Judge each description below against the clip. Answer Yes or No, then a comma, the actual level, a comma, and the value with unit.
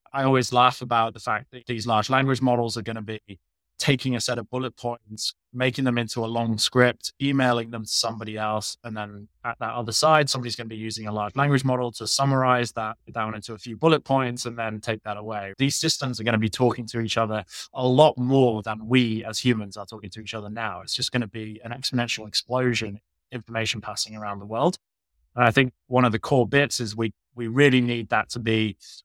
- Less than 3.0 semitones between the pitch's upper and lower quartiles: Yes, narrow, 2.5 semitones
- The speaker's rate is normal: No, fast, 235 wpm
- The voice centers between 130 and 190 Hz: No, low, 115 Hz